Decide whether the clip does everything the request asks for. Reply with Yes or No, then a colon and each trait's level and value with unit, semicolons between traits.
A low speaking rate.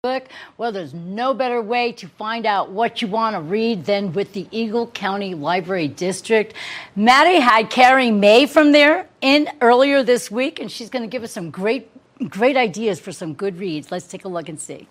No: average, 200 wpm